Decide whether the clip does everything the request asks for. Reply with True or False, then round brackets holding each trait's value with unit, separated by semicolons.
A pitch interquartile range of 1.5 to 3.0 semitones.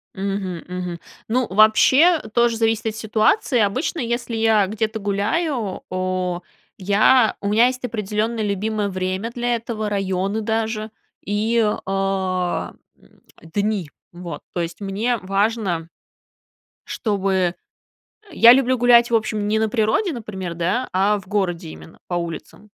False (3.4 semitones)